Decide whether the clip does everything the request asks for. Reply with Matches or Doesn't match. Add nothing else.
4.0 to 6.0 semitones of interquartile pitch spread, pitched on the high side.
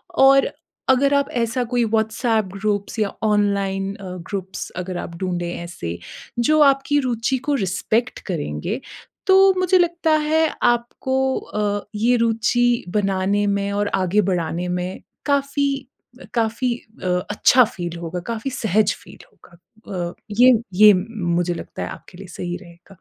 Matches